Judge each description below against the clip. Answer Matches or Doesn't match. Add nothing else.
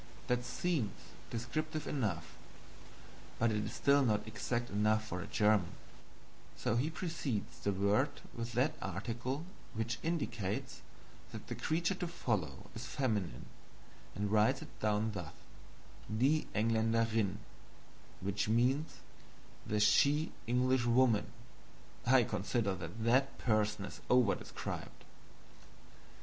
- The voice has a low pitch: Matches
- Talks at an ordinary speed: Doesn't match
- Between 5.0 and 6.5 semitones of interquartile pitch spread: Doesn't match